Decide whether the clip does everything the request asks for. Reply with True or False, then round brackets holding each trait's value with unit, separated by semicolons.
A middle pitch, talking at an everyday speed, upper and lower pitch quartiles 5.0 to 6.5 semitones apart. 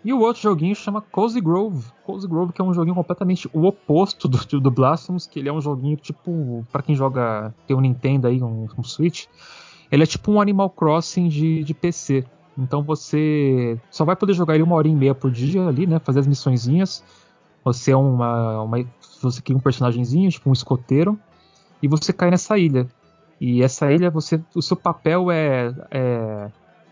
False (150 Hz; 190 wpm; 5.3 semitones)